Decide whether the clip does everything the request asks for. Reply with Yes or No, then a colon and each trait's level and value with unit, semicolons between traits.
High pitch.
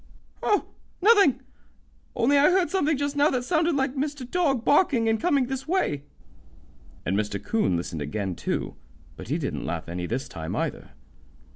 Yes: very high, 270 Hz